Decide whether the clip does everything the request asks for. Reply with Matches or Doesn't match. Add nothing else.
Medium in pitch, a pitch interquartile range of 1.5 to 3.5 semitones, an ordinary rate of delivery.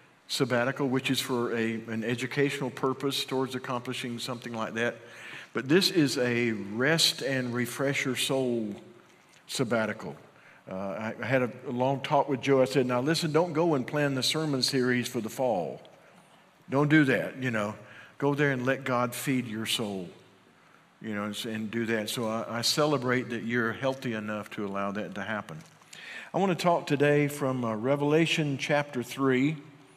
Doesn't match